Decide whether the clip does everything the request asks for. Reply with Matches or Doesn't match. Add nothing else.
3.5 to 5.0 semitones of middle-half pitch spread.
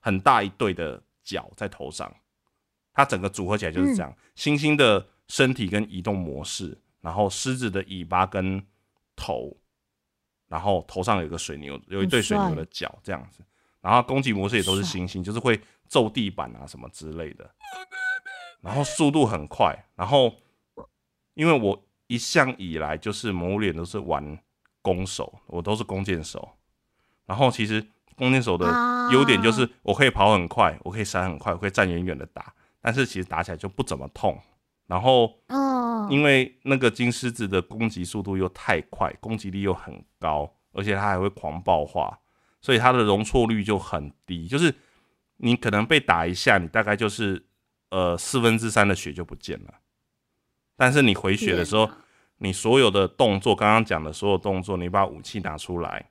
Matches